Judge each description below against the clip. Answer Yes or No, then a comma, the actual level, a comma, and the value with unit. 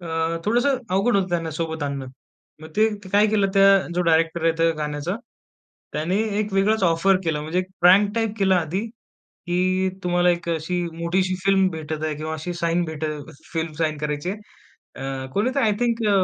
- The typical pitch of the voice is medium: Yes, medium, 175 Hz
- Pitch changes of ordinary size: Yes, average, 3.6 semitones